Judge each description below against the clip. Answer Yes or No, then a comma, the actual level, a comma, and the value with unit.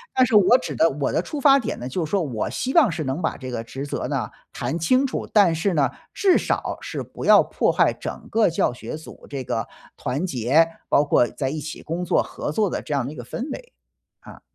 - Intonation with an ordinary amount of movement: No, wide, 7.6 semitones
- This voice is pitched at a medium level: Yes, medium, 160 Hz